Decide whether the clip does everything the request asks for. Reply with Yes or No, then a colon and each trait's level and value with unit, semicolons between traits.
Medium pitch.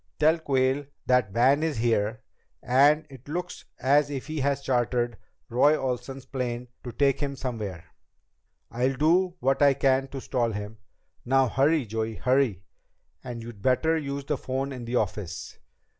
No: low, 130 Hz